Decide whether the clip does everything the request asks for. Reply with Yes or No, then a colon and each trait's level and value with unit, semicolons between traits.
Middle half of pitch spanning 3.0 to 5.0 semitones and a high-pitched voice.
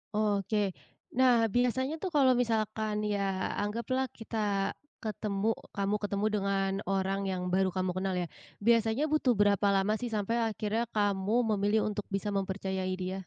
No: narrow, 2.5 semitones; high, 205 Hz